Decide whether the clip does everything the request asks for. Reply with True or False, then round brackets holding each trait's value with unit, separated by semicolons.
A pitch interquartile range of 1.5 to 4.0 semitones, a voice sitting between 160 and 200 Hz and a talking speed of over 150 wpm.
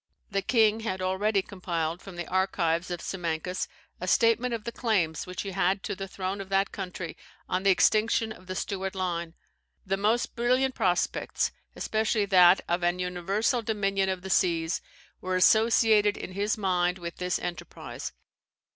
True (2.9 semitones; 190 Hz; 165 wpm)